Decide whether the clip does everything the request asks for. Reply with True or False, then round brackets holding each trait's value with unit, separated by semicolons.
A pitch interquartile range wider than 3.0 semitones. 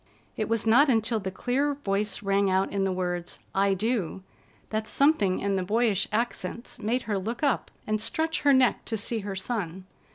True (3.6 semitones)